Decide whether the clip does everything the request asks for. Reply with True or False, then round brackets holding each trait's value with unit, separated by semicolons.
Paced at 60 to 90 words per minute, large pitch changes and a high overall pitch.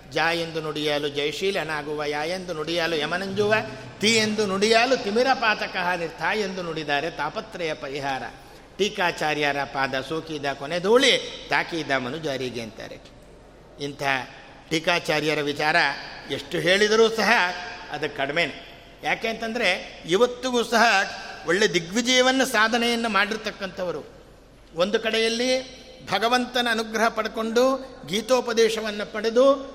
False (100 wpm; 6.9 semitones; 195 Hz)